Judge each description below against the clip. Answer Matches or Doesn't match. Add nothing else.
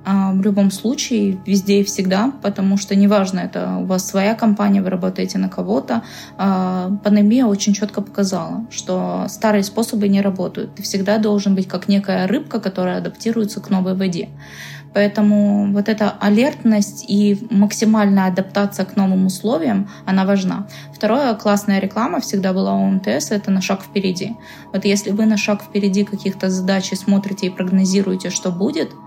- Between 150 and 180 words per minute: Matches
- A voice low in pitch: Doesn't match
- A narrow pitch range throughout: Matches